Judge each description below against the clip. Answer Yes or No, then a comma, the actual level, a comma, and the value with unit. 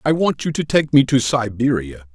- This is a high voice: No, low, 125 Hz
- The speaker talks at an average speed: No, fast, 225 wpm